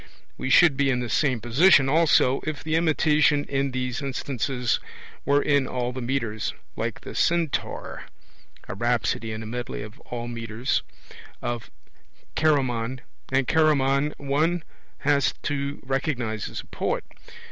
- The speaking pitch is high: No, low, 135 Hz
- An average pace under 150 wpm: Yes, average, 140 wpm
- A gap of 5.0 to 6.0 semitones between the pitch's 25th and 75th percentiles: No, average, 3.3 semitones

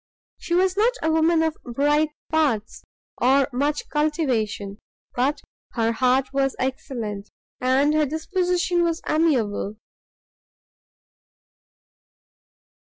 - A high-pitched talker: Yes, very high, 290 Hz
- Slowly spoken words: Yes, slow, 100 wpm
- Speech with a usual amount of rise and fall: Yes, average, 4.4 semitones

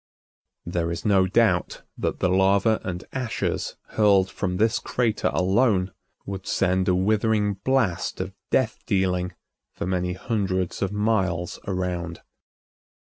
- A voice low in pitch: Yes, very low, 95 Hz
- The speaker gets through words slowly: Yes, slow, 130 wpm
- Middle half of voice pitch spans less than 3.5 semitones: Yes, narrow, 2.6 semitones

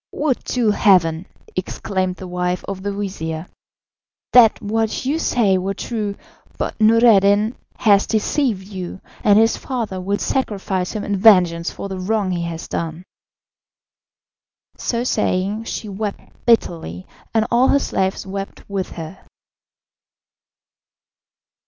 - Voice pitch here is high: Yes, high, 200 Hz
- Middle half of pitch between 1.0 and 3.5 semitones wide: Yes, average, 3.2 semitones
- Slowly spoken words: Yes, slow, 125 wpm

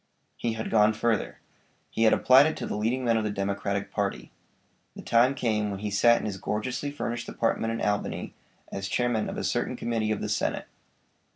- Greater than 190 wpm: Yes, average, 200 wpm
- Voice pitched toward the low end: Yes, low, 110 Hz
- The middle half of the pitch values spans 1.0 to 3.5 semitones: Yes, narrow, 2.4 semitones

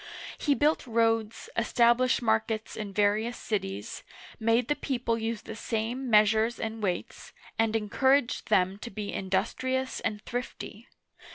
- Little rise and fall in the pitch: Yes, narrow, 2.2 semitones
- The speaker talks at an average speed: No, slow, 130 wpm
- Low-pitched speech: No, high, 225 Hz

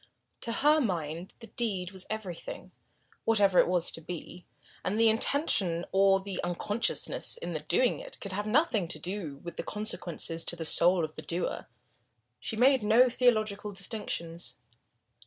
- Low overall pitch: No, high, 195 Hz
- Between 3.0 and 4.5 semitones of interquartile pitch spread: Yes, average, 4.2 semitones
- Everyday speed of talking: Yes, average, 155 wpm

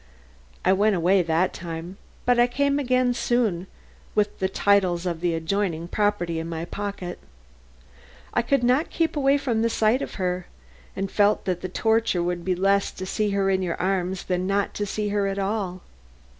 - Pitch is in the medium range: No, high, 195 Hz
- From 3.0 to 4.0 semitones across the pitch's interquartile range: Yes, average, 3.5 semitones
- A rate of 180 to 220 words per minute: Yes, average, 185 wpm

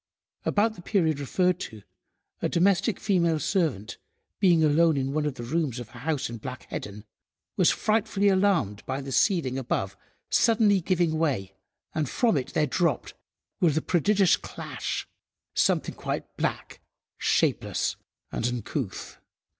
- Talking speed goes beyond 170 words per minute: No, average, 145 wpm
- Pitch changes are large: Yes, wide, 6.4 semitones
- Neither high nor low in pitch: Yes, medium, 160 Hz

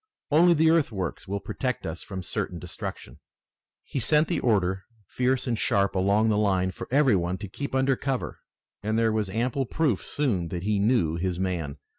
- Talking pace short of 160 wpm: No, average, 185 wpm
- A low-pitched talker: Yes, low, 105 Hz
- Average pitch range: No, wide, 5.8 semitones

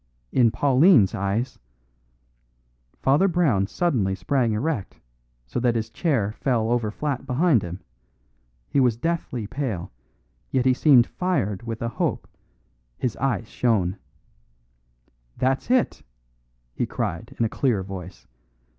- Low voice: Yes, low, 120 Hz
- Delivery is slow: Yes, slow, 130 wpm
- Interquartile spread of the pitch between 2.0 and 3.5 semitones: No, wide, 5.4 semitones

